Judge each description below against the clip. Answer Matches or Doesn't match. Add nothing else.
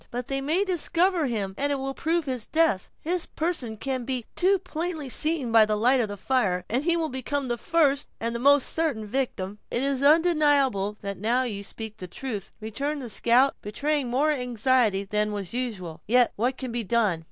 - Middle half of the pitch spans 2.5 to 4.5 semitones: Doesn't match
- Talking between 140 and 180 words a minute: Doesn't match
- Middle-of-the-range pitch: Doesn't match